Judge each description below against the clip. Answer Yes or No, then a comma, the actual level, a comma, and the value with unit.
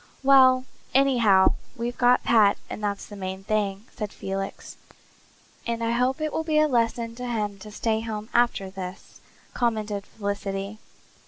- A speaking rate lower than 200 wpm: Yes, average, 155 wpm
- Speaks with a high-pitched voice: Yes, high, 220 Hz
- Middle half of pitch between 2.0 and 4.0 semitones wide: Yes, average, 3.3 semitones